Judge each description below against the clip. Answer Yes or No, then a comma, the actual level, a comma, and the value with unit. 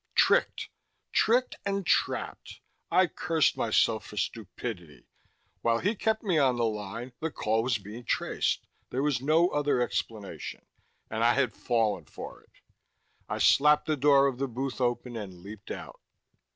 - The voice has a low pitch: Yes, low, 125 Hz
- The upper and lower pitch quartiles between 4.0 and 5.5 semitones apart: Yes, average, 5.2 semitones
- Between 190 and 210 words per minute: No, average, 155 wpm